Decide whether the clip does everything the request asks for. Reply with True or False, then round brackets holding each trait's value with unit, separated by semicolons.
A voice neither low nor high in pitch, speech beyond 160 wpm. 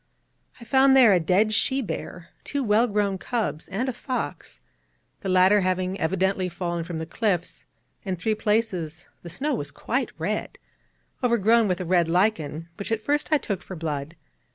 False (195 Hz; 175 wpm)